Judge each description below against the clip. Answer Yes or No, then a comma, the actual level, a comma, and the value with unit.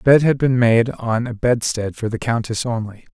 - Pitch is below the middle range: Yes, low, 115 Hz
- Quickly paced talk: Yes, fast, 230 wpm